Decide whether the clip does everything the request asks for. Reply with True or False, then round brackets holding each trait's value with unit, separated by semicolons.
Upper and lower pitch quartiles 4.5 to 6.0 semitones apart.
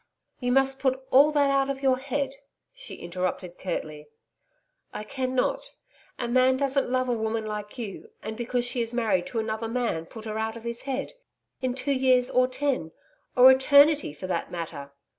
False (3.5 semitones)